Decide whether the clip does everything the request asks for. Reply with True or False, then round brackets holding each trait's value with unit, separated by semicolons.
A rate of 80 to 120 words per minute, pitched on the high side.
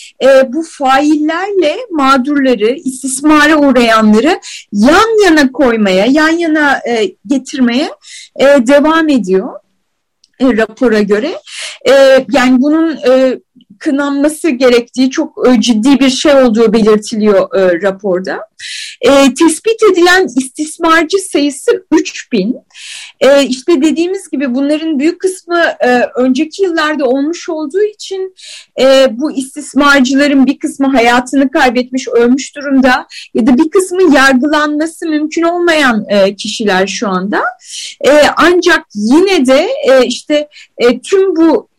True (115 wpm; 280 Hz)